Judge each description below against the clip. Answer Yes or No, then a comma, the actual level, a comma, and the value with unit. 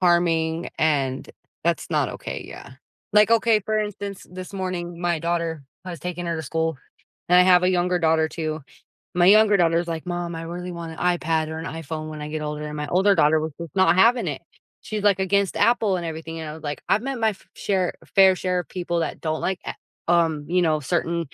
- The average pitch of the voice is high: No, medium, 175 Hz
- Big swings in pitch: No, narrow, 2.5 semitones